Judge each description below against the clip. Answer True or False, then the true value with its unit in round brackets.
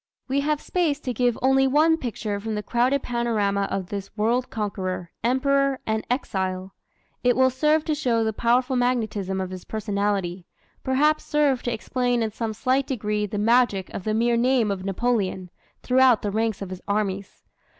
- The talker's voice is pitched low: False (230 Hz)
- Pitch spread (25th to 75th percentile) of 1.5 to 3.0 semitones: False (4.3 semitones)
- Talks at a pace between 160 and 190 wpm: True (175 wpm)